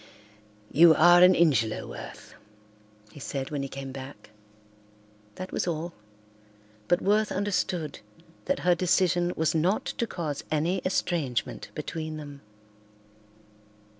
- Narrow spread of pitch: No, average, 3.8 semitones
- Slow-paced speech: Yes, slow, 120 wpm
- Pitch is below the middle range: No, medium, 165 Hz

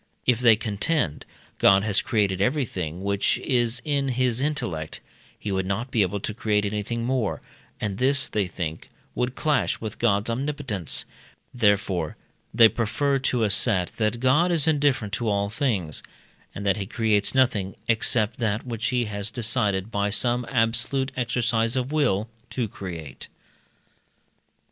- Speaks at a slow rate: No, average, 150 wpm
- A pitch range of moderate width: Yes, average, 3.9 semitones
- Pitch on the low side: Yes, low, 115 Hz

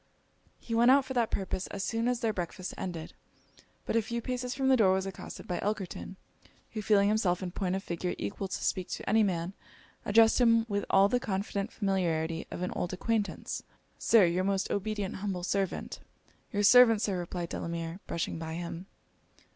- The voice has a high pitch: Yes, high, 195 Hz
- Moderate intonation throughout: Yes, average, 3.8 semitones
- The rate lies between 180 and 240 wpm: Yes, average, 185 wpm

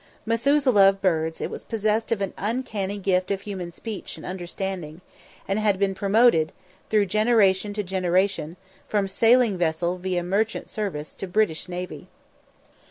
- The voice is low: No, high, 195 Hz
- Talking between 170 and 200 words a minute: No, average, 150 wpm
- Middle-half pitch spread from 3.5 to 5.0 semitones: No, average, 3.0 semitones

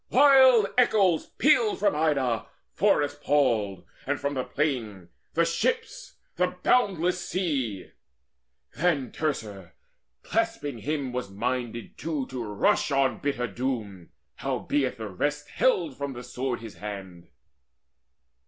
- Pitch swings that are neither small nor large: No, wide, 6.4 semitones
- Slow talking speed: Yes, slow, 120 wpm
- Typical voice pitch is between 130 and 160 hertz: Yes, medium, 140 Hz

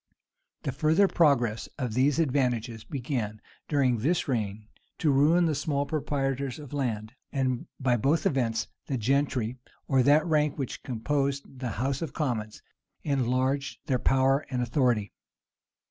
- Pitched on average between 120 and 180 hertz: Yes, low, 135 Hz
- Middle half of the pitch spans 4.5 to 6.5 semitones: No, average, 2.9 semitones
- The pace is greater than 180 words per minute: No, average, 140 wpm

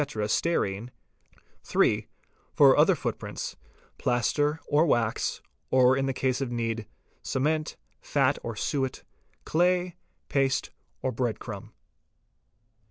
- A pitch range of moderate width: Yes, average, 3.7 semitones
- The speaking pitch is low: Yes, low, 130 Hz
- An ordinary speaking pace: No, slow, 100 wpm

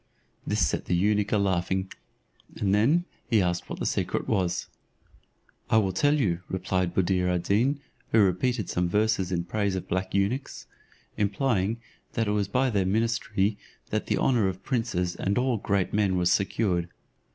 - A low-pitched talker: Yes, low, 100 Hz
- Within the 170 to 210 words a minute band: Yes, average, 175 wpm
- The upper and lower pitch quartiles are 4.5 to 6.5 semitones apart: No, average, 3.3 semitones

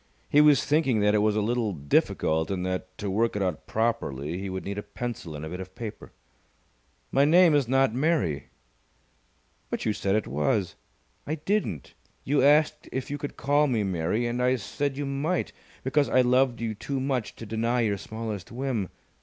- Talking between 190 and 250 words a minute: Yes, average, 195 wpm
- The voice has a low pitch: Yes, low, 115 Hz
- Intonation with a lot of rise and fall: Yes, wide, 5.8 semitones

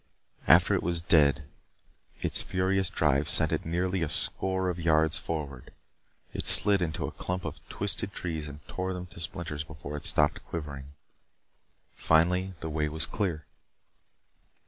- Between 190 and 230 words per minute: No, average, 150 wpm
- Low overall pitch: Yes, very low, 80 Hz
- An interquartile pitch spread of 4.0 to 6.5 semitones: No, average, 3.3 semitones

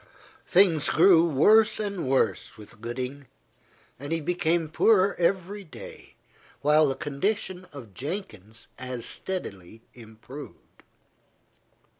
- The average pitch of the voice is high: No, medium, 155 Hz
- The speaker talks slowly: Yes, slow, 105 wpm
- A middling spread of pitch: No, wide, 6.6 semitones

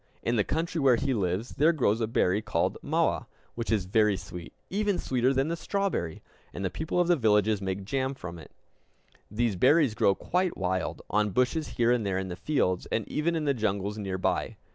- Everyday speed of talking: No, fast, 210 wpm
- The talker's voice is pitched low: Yes, low, 115 Hz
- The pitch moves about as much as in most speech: No, wide, 6.7 semitones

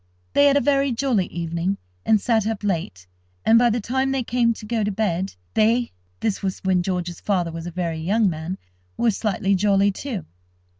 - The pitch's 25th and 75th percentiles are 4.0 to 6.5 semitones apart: Yes, average, 4.5 semitones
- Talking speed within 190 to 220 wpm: Yes, average, 195 wpm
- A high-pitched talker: Yes, high, 205 Hz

